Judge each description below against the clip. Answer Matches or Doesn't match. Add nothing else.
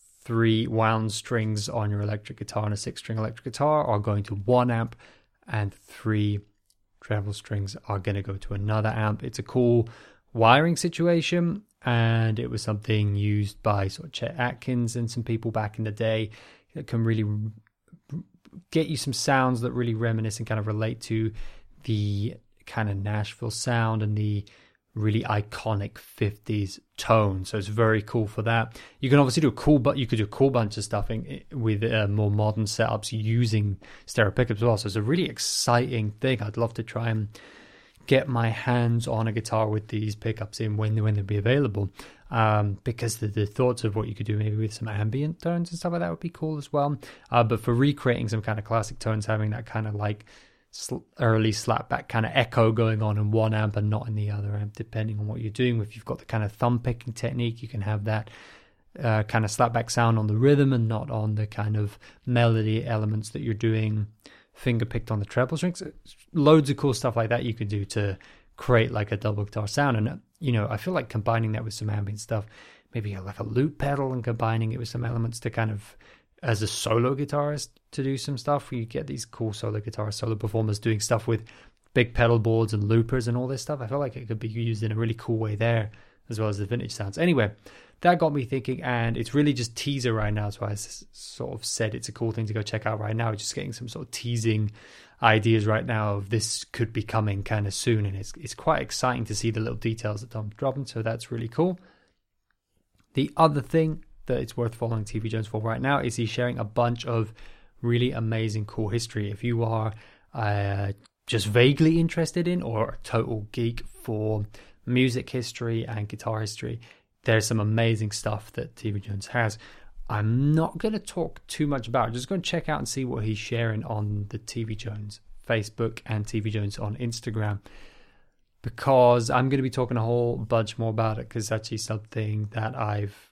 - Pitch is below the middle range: Matches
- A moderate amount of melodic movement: Doesn't match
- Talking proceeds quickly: Matches